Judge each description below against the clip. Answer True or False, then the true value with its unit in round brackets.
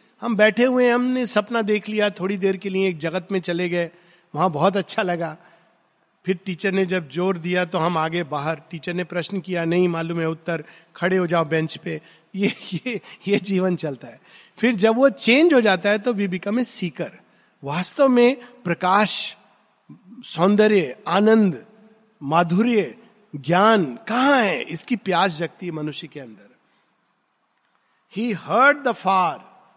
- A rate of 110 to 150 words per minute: False (160 wpm)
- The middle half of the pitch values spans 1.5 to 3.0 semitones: False (4.0 semitones)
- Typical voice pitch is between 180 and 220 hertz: True (190 Hz)